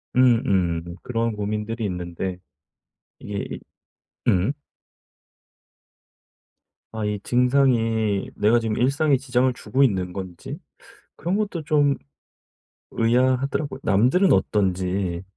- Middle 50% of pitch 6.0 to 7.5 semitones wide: No, average, 5.1 semitones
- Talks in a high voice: No, low, 115 Hz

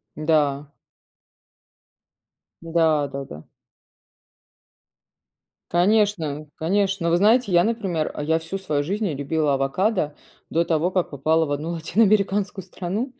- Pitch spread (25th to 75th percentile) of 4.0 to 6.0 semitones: Yes, average, 4.4 semitones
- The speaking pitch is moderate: Yes, medium, 165 Hz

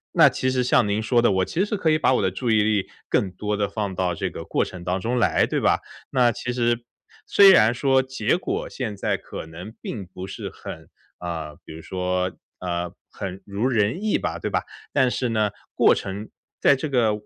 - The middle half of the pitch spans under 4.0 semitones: No, average, 5.2 semitones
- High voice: No, low, 110 Hz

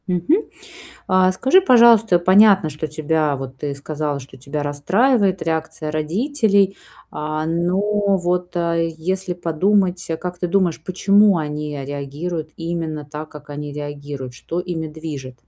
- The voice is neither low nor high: Yes, medium, 165 Hz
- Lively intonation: No, average, 3.8 semitones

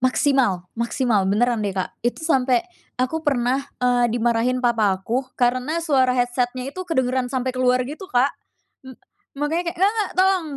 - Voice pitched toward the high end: Yes, very high, 255 Hz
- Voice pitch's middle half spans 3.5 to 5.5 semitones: No, narrow, 2.4 semitones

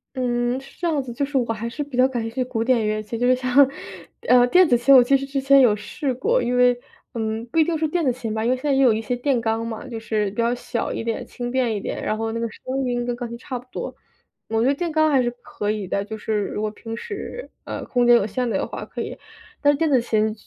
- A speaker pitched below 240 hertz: No, high, 245 Hz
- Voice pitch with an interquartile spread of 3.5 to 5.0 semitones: No, average, 3.1 semitones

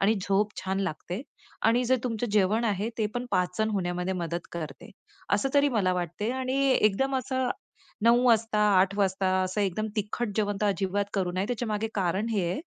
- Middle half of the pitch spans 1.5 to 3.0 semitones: No, average, 3.5 semitones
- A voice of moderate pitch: No, high, 205 Hz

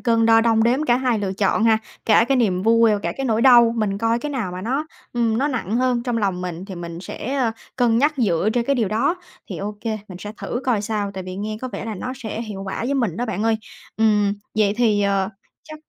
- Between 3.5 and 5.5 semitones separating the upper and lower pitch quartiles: No, average, 3.1 semitones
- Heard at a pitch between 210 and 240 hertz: Yes, high, 225 Hz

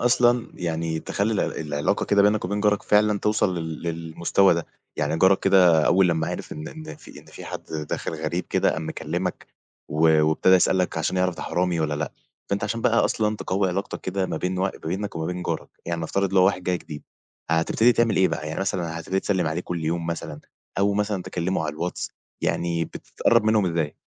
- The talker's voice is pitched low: Yes, very low, 90 Hz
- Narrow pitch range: No, average, 3.5 semitones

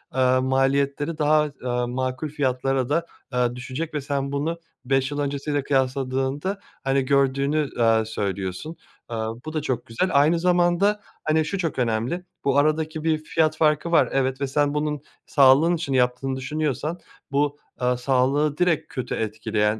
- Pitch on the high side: No, medium, 140 Hz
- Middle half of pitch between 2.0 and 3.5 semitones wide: Yes, average, 3.1 semitones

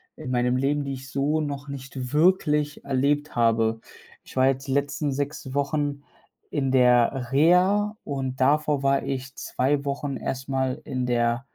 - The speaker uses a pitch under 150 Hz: Yes, low, 135 Hz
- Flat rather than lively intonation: Yes, narrow, 2.1 semitones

